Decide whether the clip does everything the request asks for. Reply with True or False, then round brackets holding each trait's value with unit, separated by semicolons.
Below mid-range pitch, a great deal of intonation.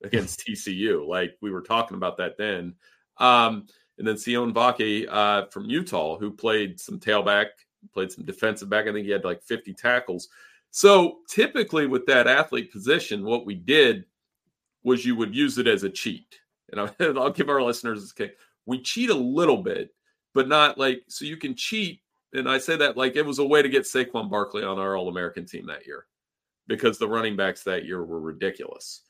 True (120 Hz; 6.5 semitones)